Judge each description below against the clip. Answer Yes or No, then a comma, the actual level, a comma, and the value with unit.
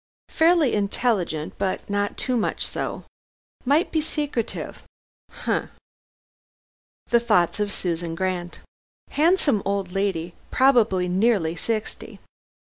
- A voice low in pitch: No, high, 205 Hz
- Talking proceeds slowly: Yes, slow, 105 wpm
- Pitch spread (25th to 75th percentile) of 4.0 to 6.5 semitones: Yes, wide, 5.5 semitones